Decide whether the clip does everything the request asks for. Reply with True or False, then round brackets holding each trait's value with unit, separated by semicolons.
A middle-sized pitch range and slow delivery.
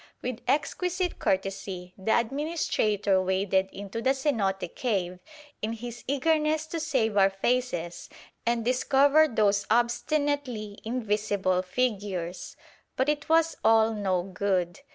False (5.7 semitones; 115 wpm)